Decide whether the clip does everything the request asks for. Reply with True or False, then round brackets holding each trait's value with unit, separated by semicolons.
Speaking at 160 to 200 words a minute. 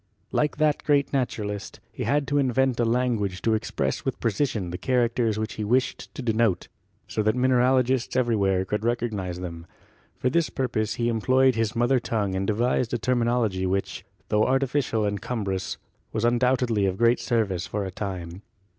True (170 wpm)